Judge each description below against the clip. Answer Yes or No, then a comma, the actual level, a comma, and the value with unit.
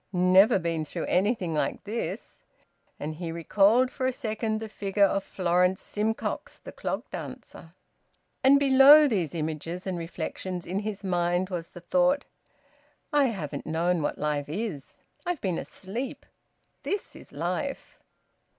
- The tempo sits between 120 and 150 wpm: Yes, average, 140 wpm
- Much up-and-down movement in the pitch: No, average, 4.9 semitones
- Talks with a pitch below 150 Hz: No, high, 190 Hz